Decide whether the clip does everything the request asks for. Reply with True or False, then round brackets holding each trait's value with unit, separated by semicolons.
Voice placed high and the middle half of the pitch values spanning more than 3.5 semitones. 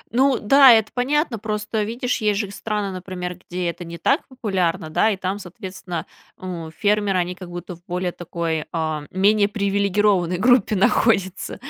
False (195 Hz; 3.2 semitones)